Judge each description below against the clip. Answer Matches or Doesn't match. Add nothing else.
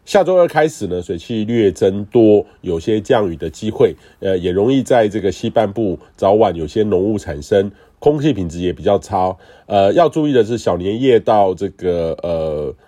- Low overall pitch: Matches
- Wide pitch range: Doesn't match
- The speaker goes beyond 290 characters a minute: Doesn't match